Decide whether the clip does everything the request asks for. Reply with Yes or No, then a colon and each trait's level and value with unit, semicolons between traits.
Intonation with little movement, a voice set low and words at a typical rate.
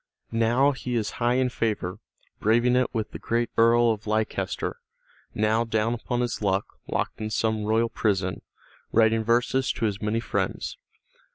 Yes: narrow, 1.7 semitones; low, 115 Hz; average, 160 wpm